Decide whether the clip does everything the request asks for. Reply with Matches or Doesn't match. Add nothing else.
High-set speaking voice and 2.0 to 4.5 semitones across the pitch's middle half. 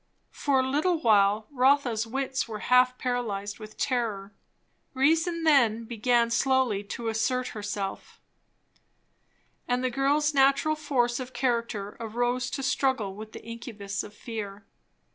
Matches